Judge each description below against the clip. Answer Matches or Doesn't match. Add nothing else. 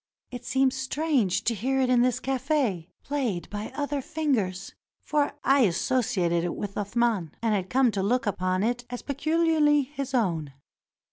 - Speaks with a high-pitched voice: Matches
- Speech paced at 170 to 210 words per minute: Doesn't match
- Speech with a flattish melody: Doesn't match